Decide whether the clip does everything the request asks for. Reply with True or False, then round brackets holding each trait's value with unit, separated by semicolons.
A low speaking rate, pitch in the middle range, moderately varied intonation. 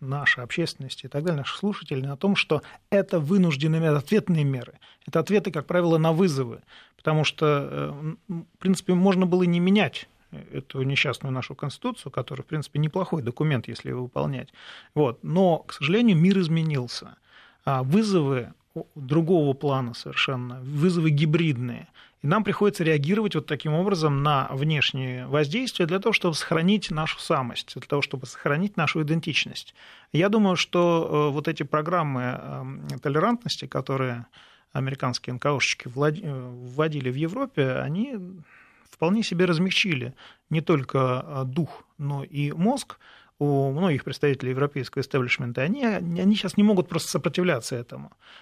False (135 wpm; 155 Hz; 4.8 semitones)